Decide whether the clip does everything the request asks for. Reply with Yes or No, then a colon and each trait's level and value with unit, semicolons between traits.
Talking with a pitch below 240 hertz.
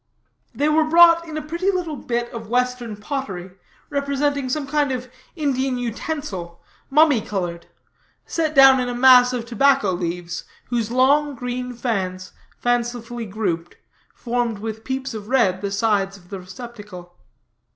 No: high, 245 Hz